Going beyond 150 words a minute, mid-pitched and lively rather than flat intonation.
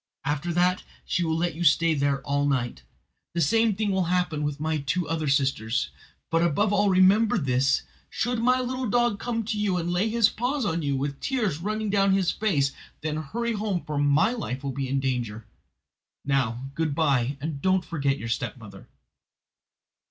Yes: average, 185 wpm; medium, 165 Hz; wide, 6.6 semitones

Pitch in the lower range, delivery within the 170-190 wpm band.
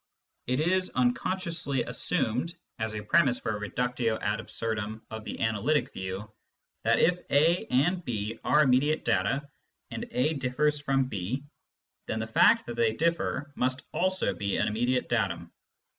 No: low, 125 Hz; average, 155 wpm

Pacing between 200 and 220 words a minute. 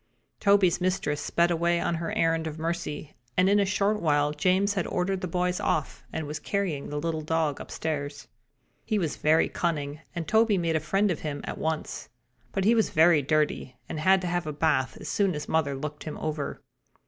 Yes: fast, 205 wpm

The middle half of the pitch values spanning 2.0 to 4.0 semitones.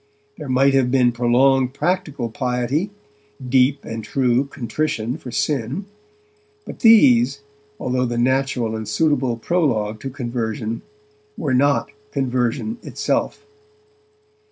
Yes: average, 2.8 semitones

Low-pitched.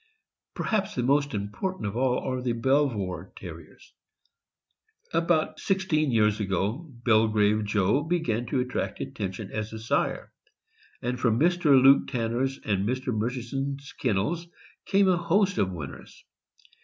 Yes: low, 125 Hz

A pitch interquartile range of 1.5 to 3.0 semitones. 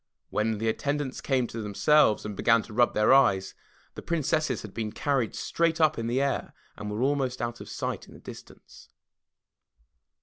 No: average, 4.6 semitones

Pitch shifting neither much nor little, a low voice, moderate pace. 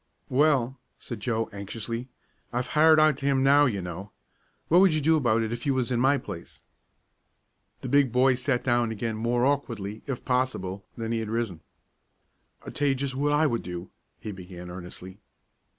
Yes: average, 4.3 semitones; low, 120 Hz; average, 185 wpm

